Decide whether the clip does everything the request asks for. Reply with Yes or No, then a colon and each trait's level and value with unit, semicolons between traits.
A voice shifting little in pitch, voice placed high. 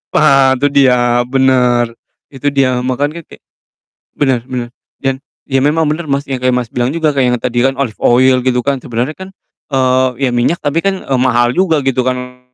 No: narrow, 2.1 semitones; low, 130 Hz